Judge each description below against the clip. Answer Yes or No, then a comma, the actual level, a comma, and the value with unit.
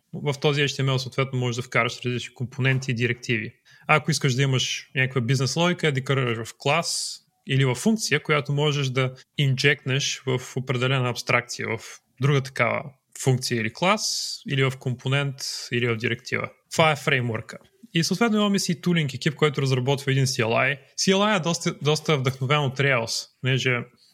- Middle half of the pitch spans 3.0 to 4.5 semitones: Yes, average, 3.3 semitones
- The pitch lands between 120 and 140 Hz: Yes, low, 135 Hz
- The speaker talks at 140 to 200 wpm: Yes, average, 160 wpm